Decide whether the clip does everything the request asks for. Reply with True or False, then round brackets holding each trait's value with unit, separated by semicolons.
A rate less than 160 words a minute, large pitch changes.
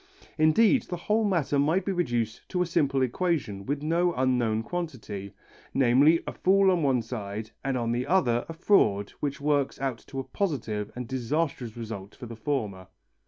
False (175 wpm; 6.4 semitones)